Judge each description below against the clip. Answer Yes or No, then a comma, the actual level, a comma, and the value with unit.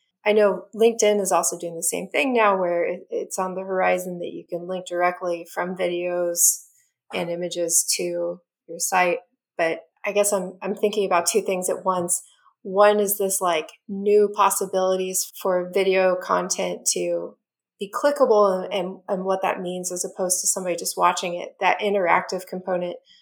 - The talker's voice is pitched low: No, medium, 185 Hz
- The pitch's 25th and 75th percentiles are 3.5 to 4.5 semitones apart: No, narrow, 2.6 semitones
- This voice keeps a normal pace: Yes, average, 170 wpm